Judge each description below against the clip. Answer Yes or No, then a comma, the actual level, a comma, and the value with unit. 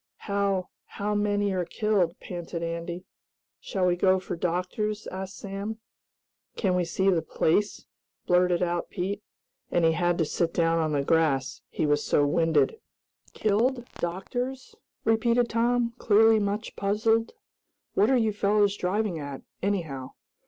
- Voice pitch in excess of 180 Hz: Yes, high, 190 Hz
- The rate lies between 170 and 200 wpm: No, average, 145 wpm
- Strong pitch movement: No, average, 3.8 semitones